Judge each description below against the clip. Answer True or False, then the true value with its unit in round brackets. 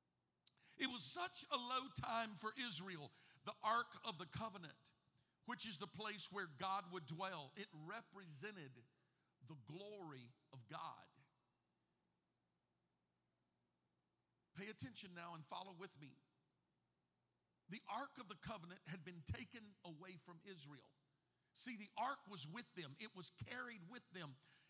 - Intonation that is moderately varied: False (6.5 semitones)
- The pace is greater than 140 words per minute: False (135 wpm)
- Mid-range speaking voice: True (180 Hz)